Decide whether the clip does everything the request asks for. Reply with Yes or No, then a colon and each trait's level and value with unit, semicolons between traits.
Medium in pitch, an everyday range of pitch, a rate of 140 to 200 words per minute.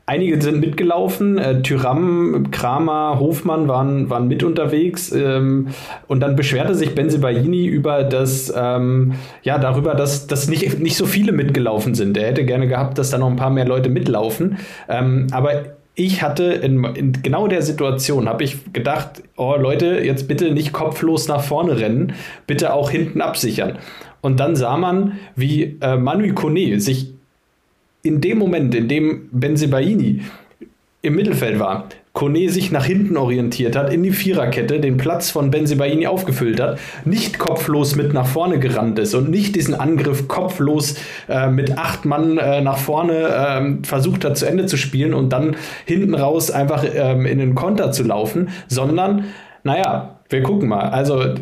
Yes: medium, 145 Hz; average, 3.8 semitones; average, 165 wpm